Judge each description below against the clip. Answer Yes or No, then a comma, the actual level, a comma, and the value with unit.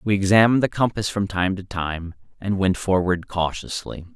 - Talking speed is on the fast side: No, average, 175 wpm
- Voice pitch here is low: Yes, very low, 95 Hz